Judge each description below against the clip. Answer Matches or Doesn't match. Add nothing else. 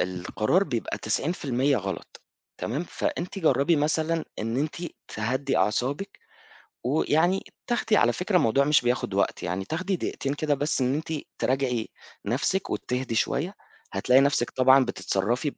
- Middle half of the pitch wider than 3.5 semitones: Matches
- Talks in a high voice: Doesn't match